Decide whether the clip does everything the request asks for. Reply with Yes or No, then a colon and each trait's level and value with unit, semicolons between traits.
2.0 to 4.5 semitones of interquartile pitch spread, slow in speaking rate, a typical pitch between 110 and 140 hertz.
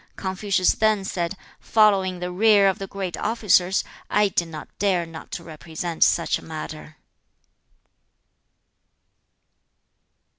No: average, 2.9 semitones; slow, 120 wpm; medium, 185 Hz